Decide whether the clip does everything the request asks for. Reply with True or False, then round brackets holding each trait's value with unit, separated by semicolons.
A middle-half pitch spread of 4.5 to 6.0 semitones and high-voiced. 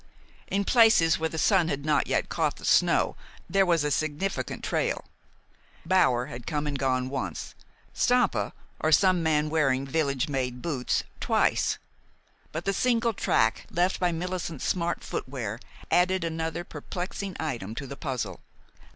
False (5.1 semitones; 160 Hz)